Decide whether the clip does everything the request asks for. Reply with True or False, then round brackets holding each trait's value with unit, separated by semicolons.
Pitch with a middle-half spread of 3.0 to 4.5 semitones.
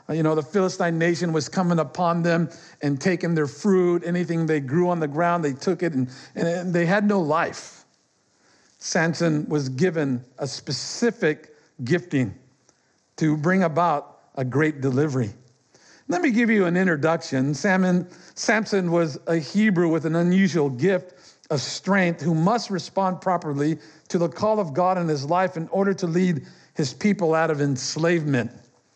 True (3.3 semitones)